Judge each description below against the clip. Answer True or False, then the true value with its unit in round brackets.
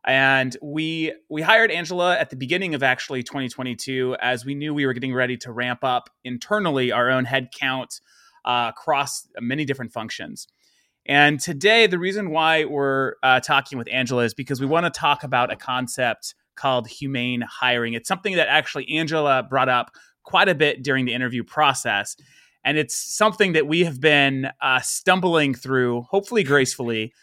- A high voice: False (135 Hz)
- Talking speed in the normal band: True (170 wpm)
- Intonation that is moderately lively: True (3.9 semitones)